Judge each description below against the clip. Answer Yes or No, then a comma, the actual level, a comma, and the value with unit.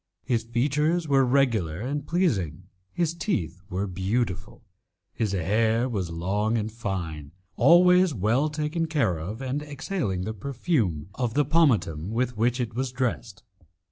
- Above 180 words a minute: No, average, 140 wpm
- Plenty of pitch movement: Yes, wide, 6.9 semitones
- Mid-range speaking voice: No, low, 115 Hz